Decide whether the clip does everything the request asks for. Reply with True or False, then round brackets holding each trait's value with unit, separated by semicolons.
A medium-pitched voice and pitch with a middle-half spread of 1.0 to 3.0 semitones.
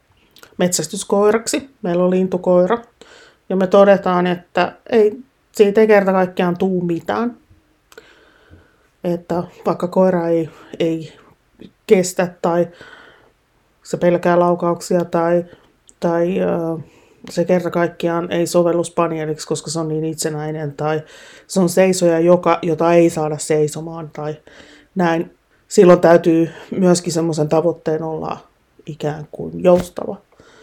True (175 Hz; 2.4 semitones)